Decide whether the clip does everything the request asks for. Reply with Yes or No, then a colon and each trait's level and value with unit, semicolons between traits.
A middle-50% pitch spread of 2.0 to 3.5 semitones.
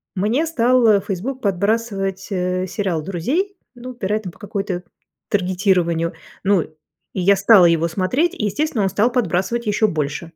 No: average, 4.1 semitones